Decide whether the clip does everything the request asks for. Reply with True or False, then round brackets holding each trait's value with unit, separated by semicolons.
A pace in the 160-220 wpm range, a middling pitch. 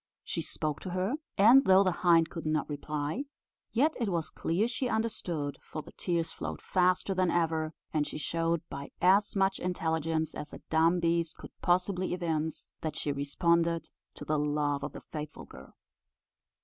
True (175 wpm; 165 Hz)